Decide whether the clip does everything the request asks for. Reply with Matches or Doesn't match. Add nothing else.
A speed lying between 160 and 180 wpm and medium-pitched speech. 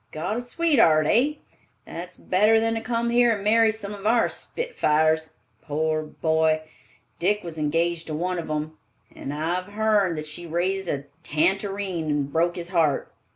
Matches